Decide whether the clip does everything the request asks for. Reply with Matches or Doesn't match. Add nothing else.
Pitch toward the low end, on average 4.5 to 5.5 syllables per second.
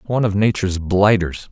Doesn't match